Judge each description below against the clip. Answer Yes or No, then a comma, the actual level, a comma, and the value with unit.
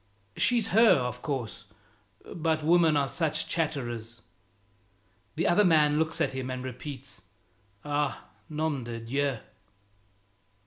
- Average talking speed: No, slow, 120 wpm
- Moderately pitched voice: Yes, medium, 145 Hz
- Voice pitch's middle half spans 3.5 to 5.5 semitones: Yes, average, 4.0 semitones